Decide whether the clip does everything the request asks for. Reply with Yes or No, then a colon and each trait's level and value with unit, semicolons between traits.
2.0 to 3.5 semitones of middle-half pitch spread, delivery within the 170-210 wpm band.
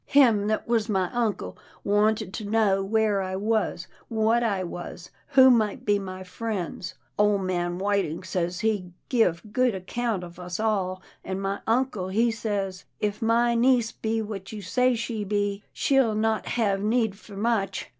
Yes: average, 3.0 semitones; average, 175 wpm